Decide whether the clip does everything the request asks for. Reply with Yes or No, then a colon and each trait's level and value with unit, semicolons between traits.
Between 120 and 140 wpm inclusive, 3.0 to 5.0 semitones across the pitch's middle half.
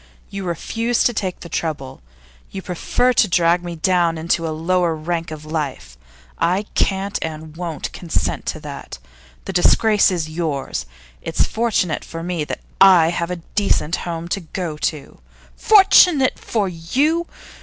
No: average, 155 wpm; average, 3.3 semitones